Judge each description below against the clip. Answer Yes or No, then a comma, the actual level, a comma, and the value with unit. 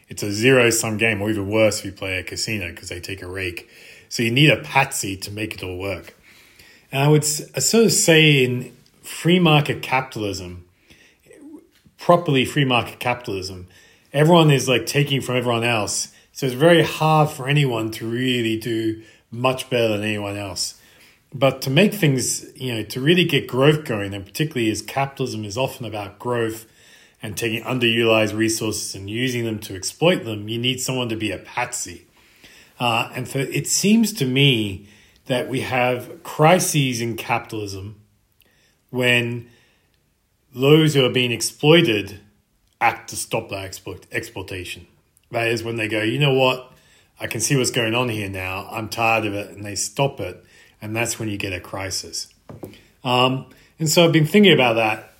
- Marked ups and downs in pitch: No, average, 4.1 semitones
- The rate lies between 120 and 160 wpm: No, average, 175 wpm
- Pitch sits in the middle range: No, low, 115 Hz